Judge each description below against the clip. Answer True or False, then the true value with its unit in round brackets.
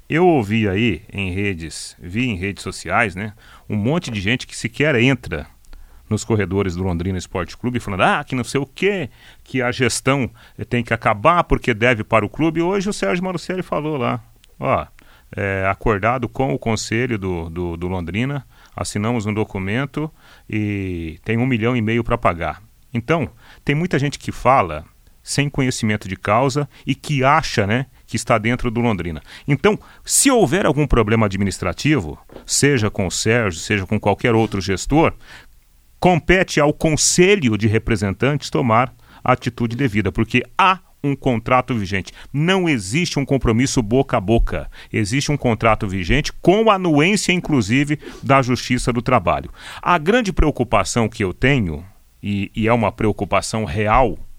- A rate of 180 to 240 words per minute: False (160 wpm)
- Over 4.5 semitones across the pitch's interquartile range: True (5.2 semitones)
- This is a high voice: False (120 Hz)